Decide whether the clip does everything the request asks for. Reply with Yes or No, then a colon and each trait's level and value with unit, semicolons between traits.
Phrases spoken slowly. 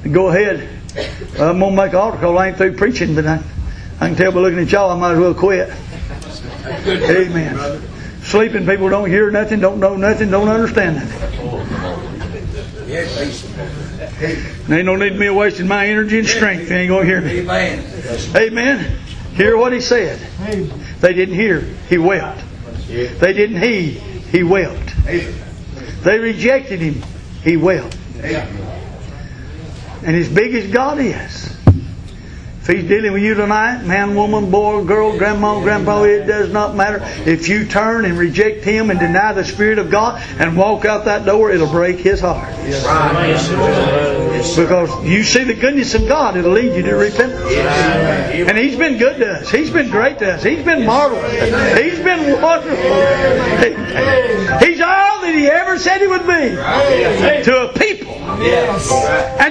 No: average, 160 wpm